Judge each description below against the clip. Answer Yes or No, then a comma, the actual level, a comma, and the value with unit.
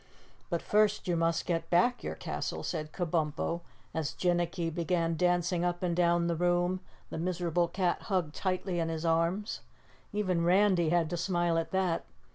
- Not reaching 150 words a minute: No, average, 165 wpm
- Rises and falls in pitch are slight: Yes, narrow, 1.5 semitones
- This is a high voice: No, medium, 175 Hz